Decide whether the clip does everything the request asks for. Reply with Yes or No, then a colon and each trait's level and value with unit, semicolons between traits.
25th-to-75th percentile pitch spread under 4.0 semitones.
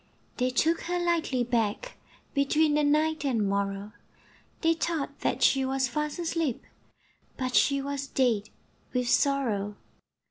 No: average, 4.4 semitones